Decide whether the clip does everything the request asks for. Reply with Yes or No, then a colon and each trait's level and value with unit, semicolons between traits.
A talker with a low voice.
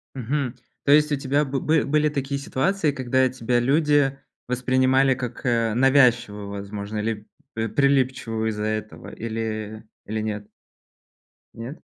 Yes: low, 125 Hz